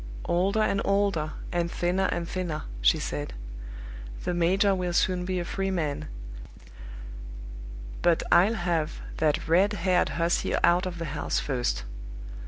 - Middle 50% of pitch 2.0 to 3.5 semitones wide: Yes, average, 2.7 semitones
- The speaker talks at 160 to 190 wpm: No, average, 140 wpm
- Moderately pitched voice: Yes, medium, 175 Hz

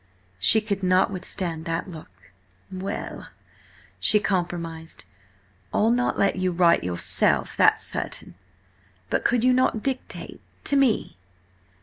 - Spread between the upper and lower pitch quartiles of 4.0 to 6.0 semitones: Yes, average, 4.9 semitones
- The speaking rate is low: Yes, slow, 115 wpm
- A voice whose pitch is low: No, medium, 185 Hz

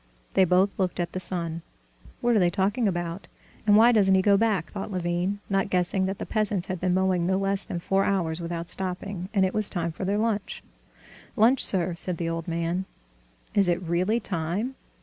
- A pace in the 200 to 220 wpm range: Yes, fast, 205 wpm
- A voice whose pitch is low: No, high, 190 Hz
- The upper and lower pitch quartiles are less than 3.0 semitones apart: Yes, narrow, 2.6 semitones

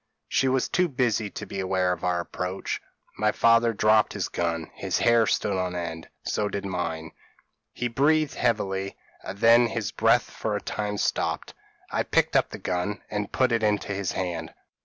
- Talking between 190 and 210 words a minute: No, average, 180 wpm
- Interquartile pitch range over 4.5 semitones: No, average, 4.2 semitones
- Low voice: Yes, low, 105 Hz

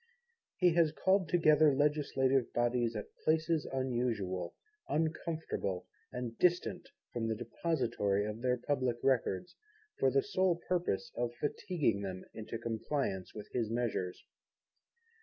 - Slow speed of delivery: Yes, slow, 120 wpm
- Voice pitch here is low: Yes, low, 125 Hz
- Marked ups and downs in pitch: Yes, wide, 6.0 semitones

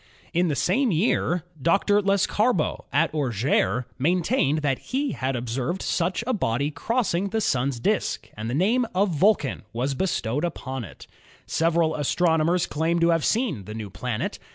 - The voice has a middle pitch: Yes, medium, 160 Hz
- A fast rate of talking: No, average, 165 wpm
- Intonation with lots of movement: Yes, wide, 6.4 semitones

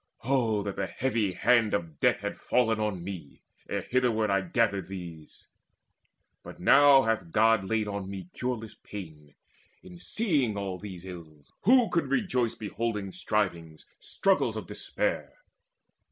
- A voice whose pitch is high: No, low, 105 Hz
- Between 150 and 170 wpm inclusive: No, average, 140 wpm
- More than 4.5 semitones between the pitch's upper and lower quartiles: Yes, average, 4.9 semitones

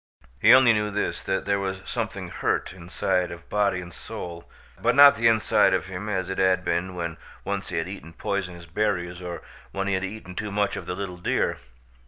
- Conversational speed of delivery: No, fast, 215 wpm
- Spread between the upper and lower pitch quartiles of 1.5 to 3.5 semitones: Yes, narrow, 2.5 semitones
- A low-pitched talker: Yes, very low, 95 Hz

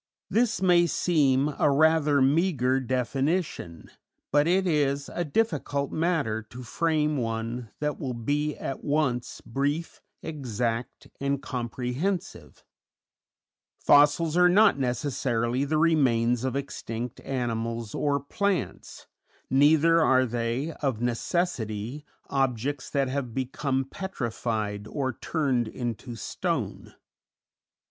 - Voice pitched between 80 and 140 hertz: Yes, low, 135 Hz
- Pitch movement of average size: Yes, average, 4.1 semitones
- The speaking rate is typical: No, slow, 105 wpm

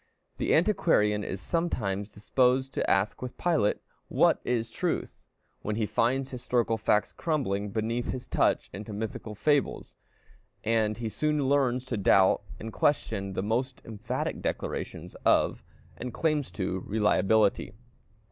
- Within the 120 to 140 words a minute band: Yes, slow, 135 wpm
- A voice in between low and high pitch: No, low, 115 Hz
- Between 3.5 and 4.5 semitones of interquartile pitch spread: Yes, average, 4.0 semitones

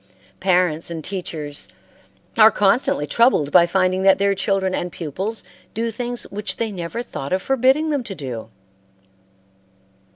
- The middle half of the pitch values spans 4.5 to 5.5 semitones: Yes, average, 4.8 semitones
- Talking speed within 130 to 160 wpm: Yes, average, 140 wpm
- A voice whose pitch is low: No, high, 190 Hz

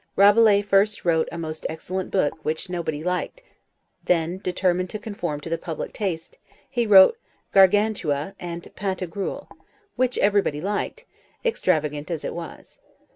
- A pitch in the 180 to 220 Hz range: Yes, medium, 185 Hz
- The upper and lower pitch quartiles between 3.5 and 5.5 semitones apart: Yes, average, 3.9 semitones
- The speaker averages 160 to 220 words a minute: No, slow, 135 wpm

